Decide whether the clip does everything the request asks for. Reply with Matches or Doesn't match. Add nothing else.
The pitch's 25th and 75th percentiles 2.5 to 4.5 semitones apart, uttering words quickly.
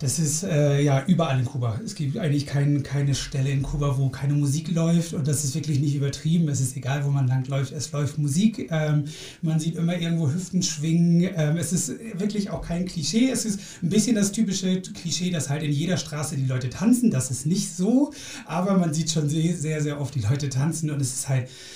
Matches